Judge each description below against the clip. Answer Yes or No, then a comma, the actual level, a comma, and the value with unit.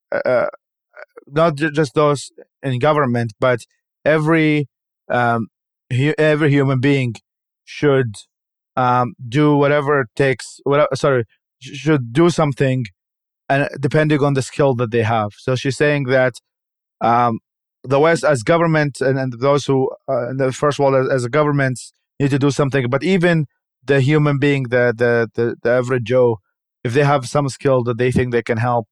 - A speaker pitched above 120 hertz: Yes, low, 135 Hz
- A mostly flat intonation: No, average, 3.0 semitones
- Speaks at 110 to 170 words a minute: Yes, average, 160 wpm